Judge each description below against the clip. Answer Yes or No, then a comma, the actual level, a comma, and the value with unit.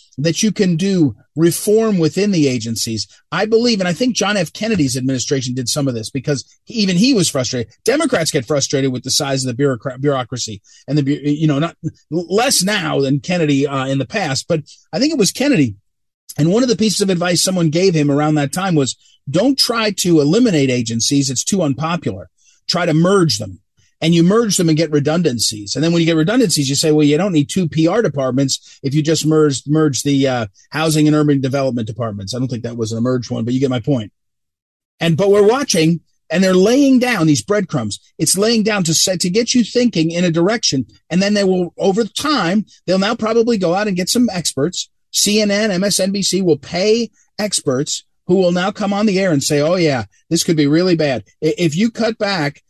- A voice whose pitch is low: No, medium, 160 Hz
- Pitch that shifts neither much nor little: No, wide, 6.1 semitones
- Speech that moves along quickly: Yes, fast, 215 wpm